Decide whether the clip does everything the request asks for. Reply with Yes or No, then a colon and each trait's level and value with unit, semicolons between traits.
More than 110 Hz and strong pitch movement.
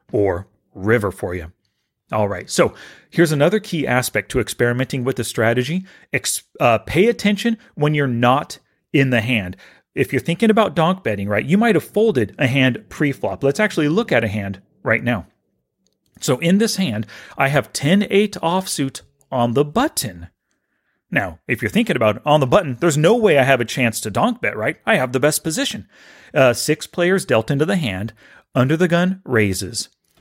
Yes: medium, 140 Hz; wide, 6.6 semitones